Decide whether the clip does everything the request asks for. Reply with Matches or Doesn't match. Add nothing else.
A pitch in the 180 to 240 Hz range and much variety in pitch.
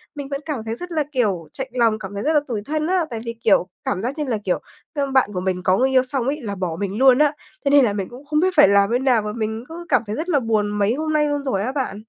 Doesn't match